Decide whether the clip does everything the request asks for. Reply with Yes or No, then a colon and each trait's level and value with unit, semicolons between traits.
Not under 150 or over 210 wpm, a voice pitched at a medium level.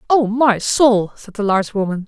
No: fast, 205 wpm; high, 220 Hz